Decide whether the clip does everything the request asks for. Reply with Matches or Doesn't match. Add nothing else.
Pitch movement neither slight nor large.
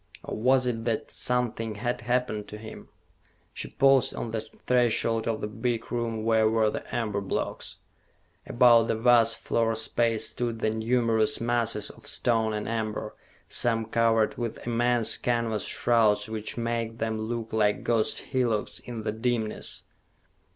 Doesn't match